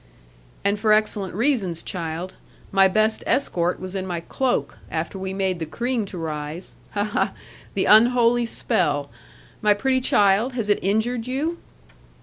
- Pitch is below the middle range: No, high, 200 Hz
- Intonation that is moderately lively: Yes, average, 4.3 semitones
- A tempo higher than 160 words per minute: No, average, 150 wpm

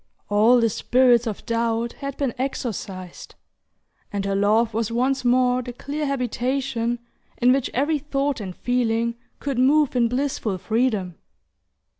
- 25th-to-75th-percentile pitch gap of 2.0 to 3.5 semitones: Yes, average, 2.7 semitones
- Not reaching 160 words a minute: Yes, average, 140 wpm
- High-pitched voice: Yes, high, 240 Hz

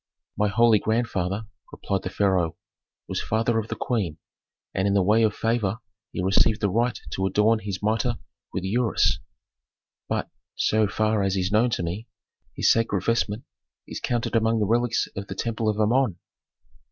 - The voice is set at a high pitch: No, low, 110 Hz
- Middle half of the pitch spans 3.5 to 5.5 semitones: No, average, 2.7 semitones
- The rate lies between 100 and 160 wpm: No, average, 175 wpm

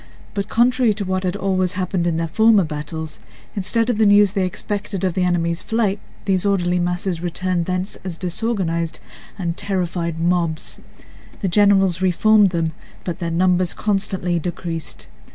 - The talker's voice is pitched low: No, medium, 185 Hz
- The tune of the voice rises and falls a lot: No, average, 2.8 semitones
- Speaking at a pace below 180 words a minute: Yes, average, 160 wpm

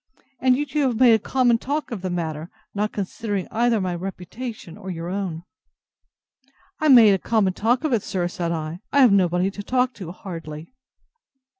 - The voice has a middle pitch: No, high, 200 Hz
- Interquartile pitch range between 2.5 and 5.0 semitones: No, wide, 5.4 semitones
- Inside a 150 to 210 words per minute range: Yes, average, 180 wpm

